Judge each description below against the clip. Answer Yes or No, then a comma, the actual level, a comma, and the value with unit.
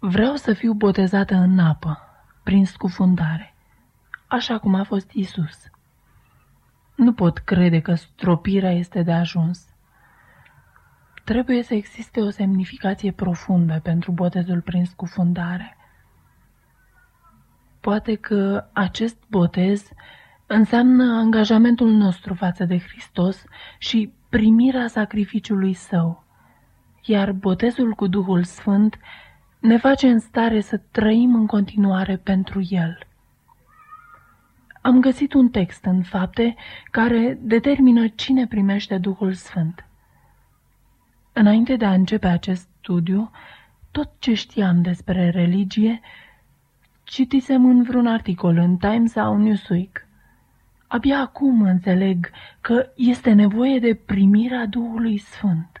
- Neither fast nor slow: No, slow, 110 wpm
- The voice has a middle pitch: No, high, 205 Hz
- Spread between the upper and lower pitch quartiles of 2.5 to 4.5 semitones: Yes, average, 3.9 semitones